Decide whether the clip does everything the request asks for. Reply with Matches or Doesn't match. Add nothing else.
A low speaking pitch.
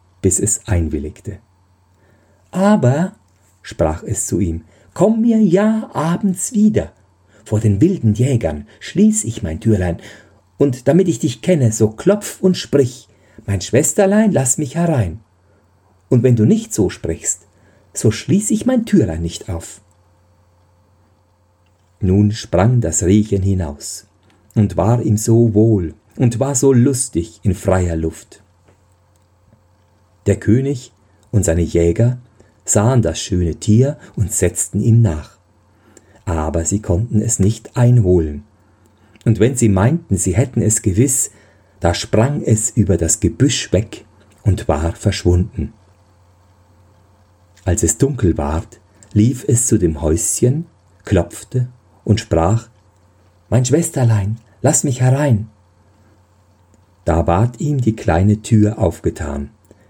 Matches